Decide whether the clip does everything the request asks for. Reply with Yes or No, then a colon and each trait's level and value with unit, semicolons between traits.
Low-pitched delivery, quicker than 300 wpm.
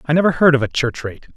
No: medium, 145 Hz; fast, 310 wpm